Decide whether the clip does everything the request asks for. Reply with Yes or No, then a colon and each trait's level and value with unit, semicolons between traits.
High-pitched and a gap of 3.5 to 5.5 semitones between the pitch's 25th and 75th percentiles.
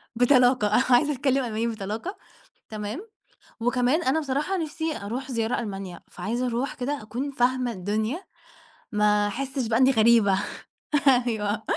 Yes: high, 245 Hz; average, 3.9 semitones